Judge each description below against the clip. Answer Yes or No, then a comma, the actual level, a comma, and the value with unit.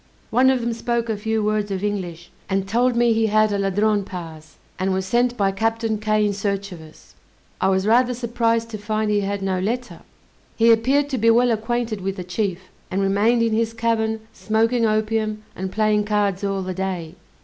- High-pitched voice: Yes, high, 215 Hz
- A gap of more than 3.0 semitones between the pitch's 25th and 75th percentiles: No, average, 2.7 semitones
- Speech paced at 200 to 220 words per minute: Yes, fast, 205 wpm